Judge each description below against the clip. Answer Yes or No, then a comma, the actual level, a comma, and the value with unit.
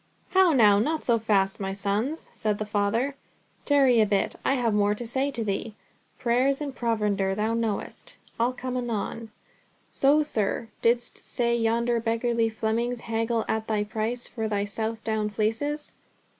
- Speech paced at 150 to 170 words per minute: Yes, average, 155 wpm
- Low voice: No, high, 225 Hz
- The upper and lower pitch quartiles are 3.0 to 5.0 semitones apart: No, narrow, 2.6 semitones